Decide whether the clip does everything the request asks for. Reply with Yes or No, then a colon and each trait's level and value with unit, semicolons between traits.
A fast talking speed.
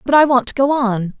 Yes: fast, 300 wpm